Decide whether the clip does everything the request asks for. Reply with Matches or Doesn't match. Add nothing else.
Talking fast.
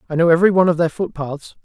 Matches